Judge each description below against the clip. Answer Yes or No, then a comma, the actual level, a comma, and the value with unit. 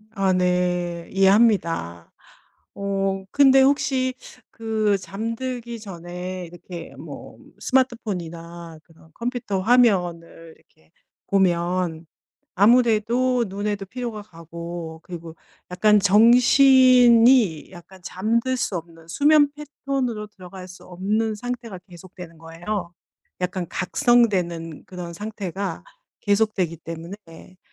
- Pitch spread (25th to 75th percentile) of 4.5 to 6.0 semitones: Yes, average, 5.1 semitones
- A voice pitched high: Yes, high, 195 Hz